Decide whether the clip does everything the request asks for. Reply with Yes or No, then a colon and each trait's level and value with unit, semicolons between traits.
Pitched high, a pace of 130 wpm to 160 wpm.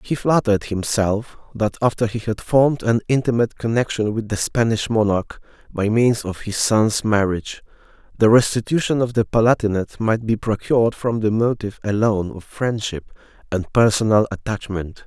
No: low, 110 Hz; average, 150 wpm